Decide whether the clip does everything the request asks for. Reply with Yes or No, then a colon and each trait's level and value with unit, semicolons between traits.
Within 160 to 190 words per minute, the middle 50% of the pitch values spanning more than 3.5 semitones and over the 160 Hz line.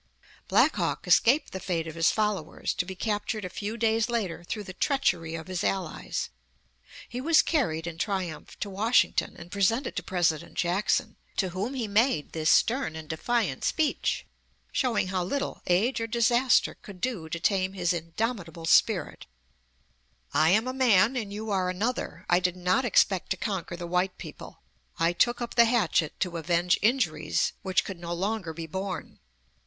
Yes: average, 175 wpm; average, 4.8 semitones; high, 190 Hz